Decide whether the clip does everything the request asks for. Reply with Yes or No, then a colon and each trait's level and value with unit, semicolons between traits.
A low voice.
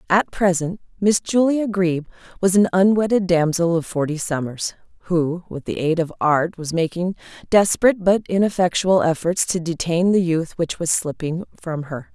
No: medium, 175 Hz